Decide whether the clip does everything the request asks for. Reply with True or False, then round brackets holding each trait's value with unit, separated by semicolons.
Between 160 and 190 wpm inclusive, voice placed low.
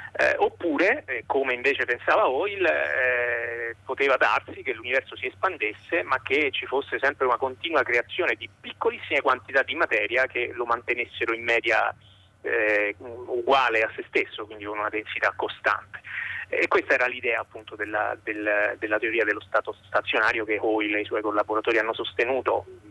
True (165 wpm; 120 Hz)